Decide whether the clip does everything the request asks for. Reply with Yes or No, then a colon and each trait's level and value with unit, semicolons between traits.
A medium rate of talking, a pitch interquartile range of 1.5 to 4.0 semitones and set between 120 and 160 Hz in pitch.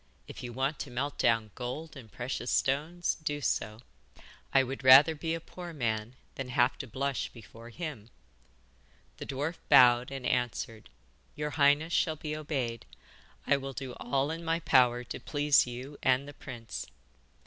Yes: average, 165 wpm; average, 3.4 semitones; low, 135 Hz